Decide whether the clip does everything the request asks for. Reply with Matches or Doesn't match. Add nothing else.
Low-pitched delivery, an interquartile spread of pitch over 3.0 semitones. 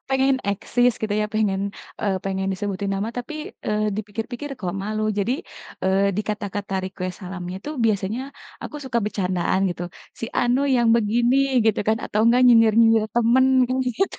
Doesn't match